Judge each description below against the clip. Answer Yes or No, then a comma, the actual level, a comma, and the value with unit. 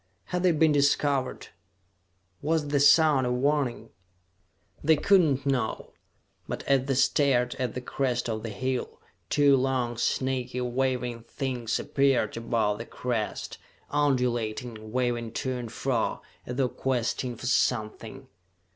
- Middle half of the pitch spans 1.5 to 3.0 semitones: Yes, narrow, 2.5 semitones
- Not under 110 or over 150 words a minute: Yes, slow, 135 wpm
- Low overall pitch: Yes, low, 130 Hz